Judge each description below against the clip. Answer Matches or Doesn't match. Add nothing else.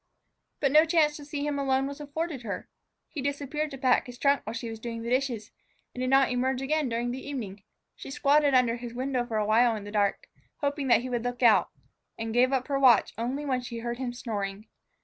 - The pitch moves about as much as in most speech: Matches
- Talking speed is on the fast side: Matches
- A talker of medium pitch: Doesn't match